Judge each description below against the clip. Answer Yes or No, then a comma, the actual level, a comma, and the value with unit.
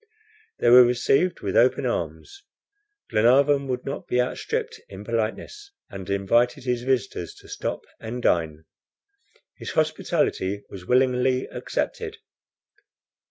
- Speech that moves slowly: Yes, slow, 115 wpm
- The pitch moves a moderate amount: Yes, average, 4.3 semitones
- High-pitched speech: No, low, 125 Hz